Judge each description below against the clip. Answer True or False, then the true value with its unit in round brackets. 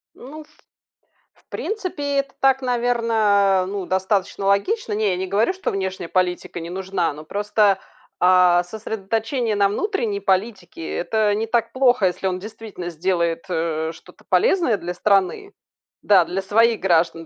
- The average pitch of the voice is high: True (200 Hz)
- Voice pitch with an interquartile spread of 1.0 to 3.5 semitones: False (4.1 semitones)